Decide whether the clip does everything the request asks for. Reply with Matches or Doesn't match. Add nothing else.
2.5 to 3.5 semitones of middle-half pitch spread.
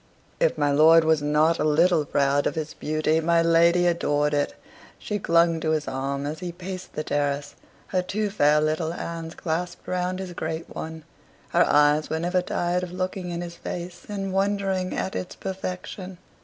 Matches